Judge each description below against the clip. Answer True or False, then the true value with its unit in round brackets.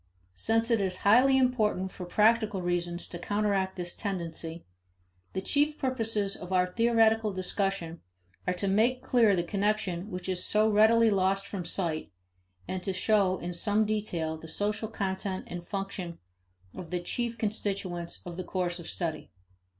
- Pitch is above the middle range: True (195 Hz)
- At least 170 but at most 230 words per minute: True (175 wpm)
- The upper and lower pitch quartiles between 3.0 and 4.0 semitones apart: True (3.4 semitones)